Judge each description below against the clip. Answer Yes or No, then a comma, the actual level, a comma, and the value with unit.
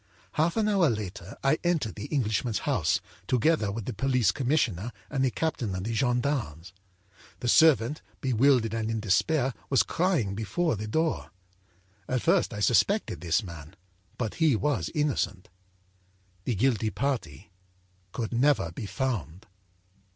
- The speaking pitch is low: Yes, low, 120 Hz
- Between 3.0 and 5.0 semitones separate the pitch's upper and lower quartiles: No, wide, 5.5 semitones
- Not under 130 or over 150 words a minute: Yes, average, 145 wpm